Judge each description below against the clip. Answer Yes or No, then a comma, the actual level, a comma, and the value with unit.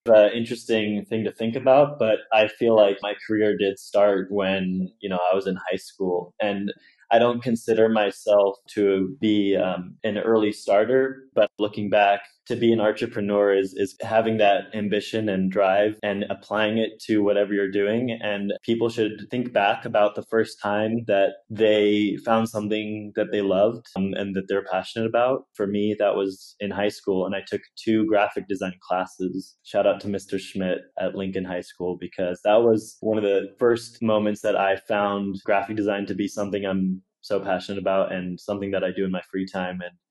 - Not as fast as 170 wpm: No, average, 195 wpm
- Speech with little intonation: Yes, narrow, 2.1 semitones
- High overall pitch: No, low, 105 Hz